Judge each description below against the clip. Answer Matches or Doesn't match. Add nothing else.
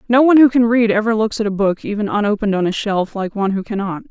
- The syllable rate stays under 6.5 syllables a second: Doesn't match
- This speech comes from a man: Doesn't match